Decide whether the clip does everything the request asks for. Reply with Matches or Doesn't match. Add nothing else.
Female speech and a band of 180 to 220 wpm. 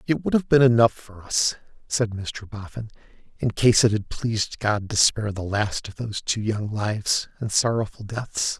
Doesn't match